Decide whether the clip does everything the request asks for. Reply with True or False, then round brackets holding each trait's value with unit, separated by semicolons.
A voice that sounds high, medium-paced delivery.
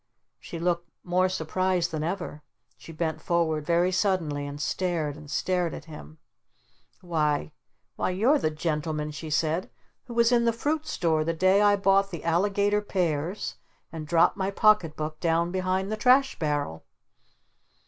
False (170 Hz; 160 wpm)